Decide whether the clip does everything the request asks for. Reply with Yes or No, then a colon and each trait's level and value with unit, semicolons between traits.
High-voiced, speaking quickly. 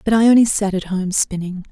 Yes: high, 200 Hz; fast, 210 wpm